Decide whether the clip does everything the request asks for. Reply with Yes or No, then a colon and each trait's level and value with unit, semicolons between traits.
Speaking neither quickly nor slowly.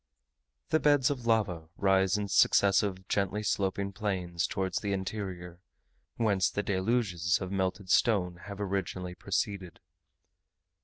No: slow, 120 wpm